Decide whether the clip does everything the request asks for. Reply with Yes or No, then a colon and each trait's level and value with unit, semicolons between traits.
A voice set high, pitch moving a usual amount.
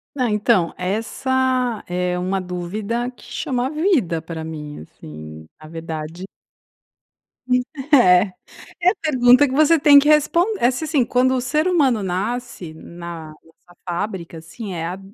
No: high, 210 Hz; wide, 7.2 semitones